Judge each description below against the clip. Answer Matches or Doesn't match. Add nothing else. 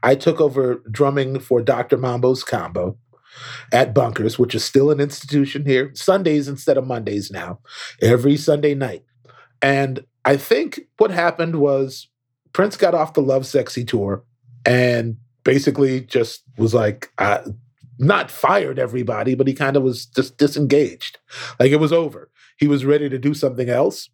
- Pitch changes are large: Doesn't match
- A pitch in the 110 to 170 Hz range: Matches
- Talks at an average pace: Matches